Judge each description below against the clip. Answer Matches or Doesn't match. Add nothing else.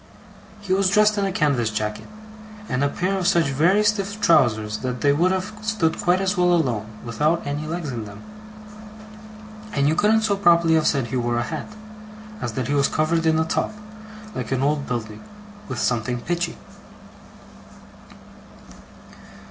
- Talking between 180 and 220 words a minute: Doesn't match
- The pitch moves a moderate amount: Doesn't match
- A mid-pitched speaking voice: Matches